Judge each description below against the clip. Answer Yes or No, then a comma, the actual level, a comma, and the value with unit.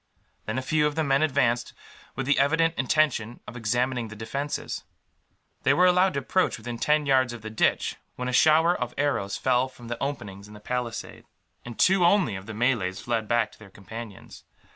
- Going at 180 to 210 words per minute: Yes, average, 200 wpm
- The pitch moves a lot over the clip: No, average, 4.4 semitones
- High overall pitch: No, low, 125 Hz